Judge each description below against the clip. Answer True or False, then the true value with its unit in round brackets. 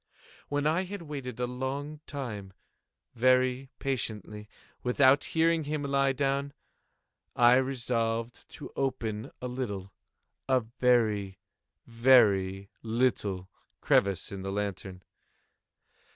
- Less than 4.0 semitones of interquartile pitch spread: False (4.6 semitones)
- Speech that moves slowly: True (100 wpm)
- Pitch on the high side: False (125 Hz)